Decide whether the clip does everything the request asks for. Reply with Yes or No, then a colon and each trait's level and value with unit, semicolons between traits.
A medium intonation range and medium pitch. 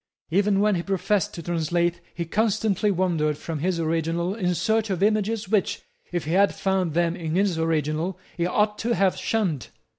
Yes: average, 3.6 semitones; medium, 180 Hz